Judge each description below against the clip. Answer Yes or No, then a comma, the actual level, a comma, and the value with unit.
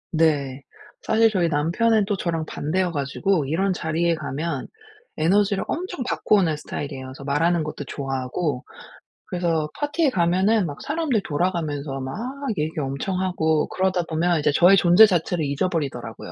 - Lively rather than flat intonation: No, average, 4.4 semitones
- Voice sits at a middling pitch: Yes, medium, 165 Hz